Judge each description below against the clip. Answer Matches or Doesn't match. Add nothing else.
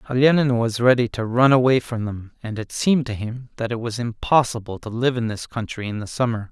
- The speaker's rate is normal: Doesn't match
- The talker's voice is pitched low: Matches